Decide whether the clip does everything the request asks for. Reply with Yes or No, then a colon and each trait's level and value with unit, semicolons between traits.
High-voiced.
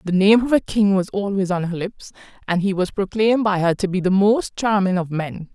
Yes: high, 195 Hz